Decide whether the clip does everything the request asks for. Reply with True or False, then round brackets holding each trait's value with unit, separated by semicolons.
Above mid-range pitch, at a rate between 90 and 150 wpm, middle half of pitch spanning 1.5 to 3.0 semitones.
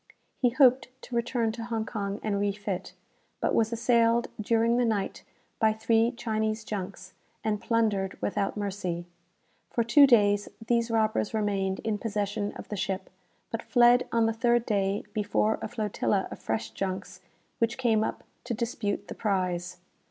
False (220 Hz; 160 wpm; 2.5 semitones)